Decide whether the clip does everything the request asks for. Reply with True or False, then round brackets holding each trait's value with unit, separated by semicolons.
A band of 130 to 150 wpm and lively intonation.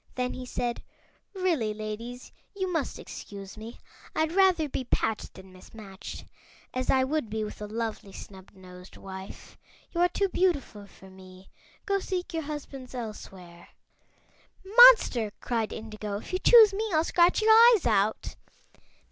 True (145 wpm; 9.0 semitones)